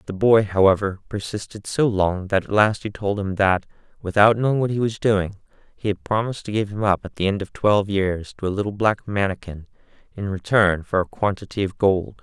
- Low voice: Yes, low, 100 Hz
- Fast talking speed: Yes, fast, 215 wpm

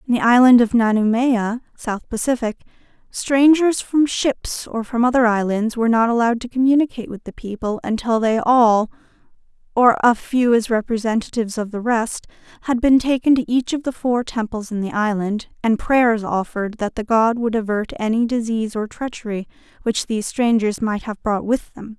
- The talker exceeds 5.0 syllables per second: Yes, 5.2 syllables/s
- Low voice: No, high, 230 Hz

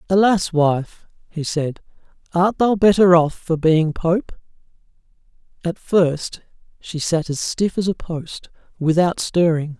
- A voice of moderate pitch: Yes, medium, 170 Hz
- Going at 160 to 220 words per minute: No, slow, 135 wpm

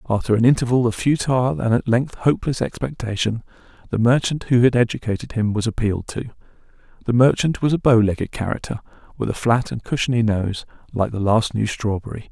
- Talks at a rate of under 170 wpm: No, average, 180 wpm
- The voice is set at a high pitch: No, low, 115 Hz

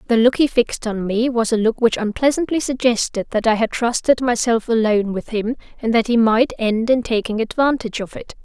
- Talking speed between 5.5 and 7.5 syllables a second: Yes, 5.6 syllables/s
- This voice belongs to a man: No, female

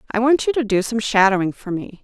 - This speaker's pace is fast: Yes, fast, 265 wpm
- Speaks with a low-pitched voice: No, high, 220 Hz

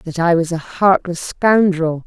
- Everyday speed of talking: Yes, average, 175 wpm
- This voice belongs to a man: No, female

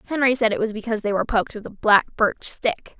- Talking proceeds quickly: Yes, fast, 260 wpm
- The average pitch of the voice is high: Yes, high, 220 Hz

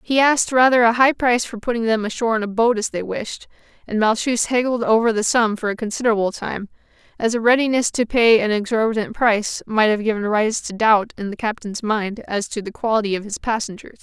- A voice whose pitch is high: Yes, high, 225 Hz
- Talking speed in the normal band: No, fast, 220 wpm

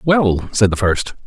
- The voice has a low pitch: Yes, low, 115 Hz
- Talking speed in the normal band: Yes, average, 190 wpm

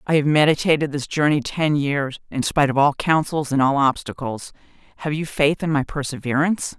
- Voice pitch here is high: No, medium, 145 Hz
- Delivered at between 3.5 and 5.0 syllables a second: No, 5.5 syllables/s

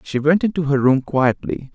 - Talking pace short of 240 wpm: Yes, fast, 205 wpm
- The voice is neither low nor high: Yes, medium, 145 Hz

